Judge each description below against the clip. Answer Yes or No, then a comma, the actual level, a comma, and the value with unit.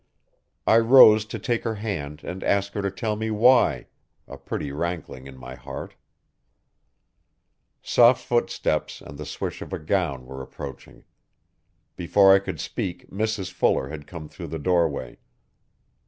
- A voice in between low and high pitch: No, very low, 95 Hz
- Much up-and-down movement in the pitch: Yes, wide, 6.5 semitones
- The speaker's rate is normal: Yes, average, 150 wpm